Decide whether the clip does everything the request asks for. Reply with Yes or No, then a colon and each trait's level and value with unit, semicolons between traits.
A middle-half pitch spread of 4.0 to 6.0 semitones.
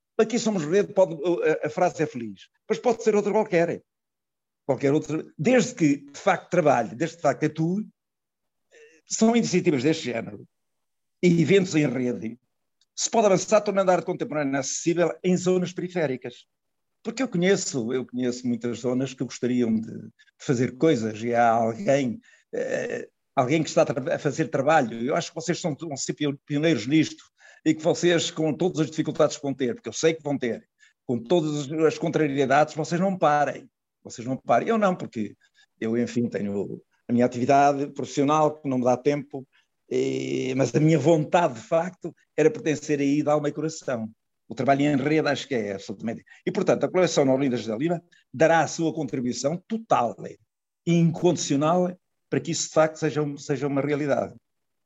Yes: average, 4.5 semitones